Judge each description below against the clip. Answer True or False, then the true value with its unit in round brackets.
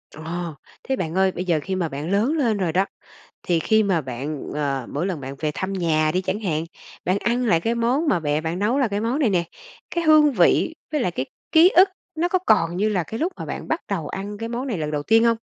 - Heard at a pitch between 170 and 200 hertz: True (190 Hz)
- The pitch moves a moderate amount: False (6.3 semitones)